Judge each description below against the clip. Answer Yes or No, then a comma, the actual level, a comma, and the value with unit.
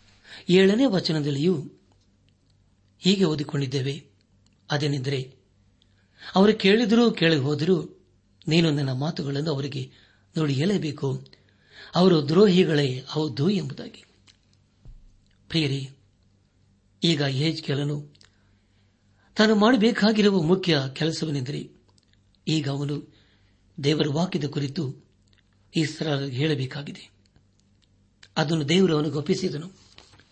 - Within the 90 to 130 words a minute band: No, average, 75 wpm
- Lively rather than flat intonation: Yes, wide, 8.2 semitones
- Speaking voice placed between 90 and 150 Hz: Yes, medium, 140 Hz